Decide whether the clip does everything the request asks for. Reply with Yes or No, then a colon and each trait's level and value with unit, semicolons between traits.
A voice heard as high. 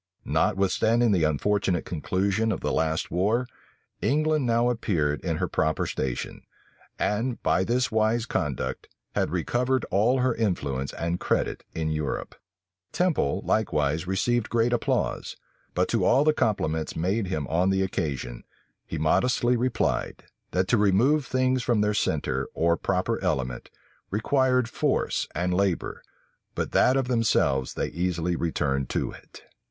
No: very low, 95 Hz